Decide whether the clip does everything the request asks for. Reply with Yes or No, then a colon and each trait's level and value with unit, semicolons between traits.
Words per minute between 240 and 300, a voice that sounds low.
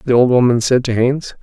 Yes: fast, 250 wpm; low, 125 Hz